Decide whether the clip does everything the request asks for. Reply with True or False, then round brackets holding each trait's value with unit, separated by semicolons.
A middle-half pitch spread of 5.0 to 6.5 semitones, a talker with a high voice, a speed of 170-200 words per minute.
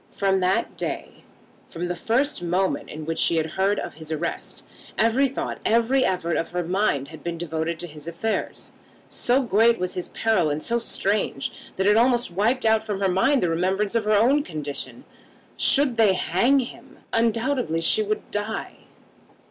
True (5.3 semitones; 195 Hz; 180 wpm)